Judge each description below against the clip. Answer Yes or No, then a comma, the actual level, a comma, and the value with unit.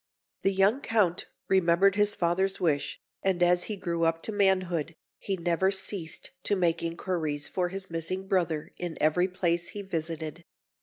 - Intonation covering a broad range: No, narrow, 2.4 semitones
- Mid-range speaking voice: Yes, medium, 175 Hz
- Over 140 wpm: Yes, average, 160 wpm